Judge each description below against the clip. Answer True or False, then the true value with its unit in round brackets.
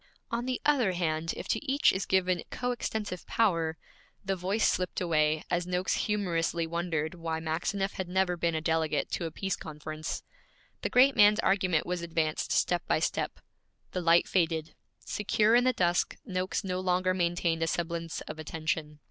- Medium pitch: True (175 Hz)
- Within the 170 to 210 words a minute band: True (175 wpm)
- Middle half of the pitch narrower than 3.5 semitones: True (2.9 semitones)